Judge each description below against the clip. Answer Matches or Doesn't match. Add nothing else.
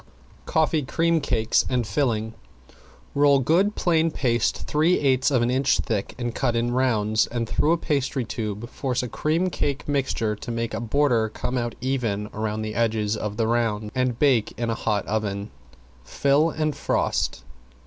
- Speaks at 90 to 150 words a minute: Doesn't match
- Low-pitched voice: Matches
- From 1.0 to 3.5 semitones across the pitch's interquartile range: Doesn't match